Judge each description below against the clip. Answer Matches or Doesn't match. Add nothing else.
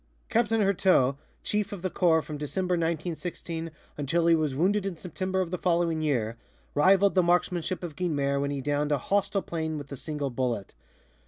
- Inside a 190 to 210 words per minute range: Doesn't match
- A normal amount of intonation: Matches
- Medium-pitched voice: Matches